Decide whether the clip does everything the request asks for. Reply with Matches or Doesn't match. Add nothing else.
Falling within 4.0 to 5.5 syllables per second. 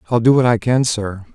Doesn't match